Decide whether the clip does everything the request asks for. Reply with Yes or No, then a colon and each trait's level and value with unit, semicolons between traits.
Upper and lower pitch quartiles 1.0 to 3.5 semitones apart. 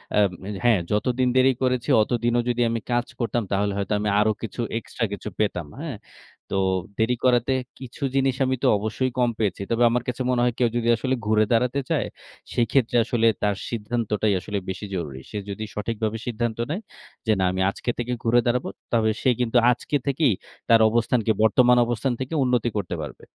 Yes: narrow, 2.6 semitones